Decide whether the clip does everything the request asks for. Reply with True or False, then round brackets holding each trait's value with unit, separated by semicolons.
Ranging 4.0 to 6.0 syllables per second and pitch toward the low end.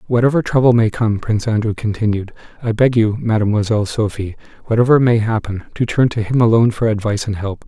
False (6.4 syllables/s; 110 Hz)